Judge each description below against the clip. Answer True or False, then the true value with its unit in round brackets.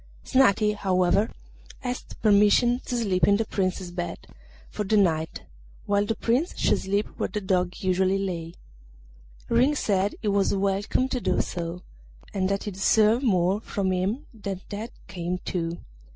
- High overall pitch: True (200 Hz)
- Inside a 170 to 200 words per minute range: False (155 wpm)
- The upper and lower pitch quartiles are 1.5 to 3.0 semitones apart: True (2.7 semitones)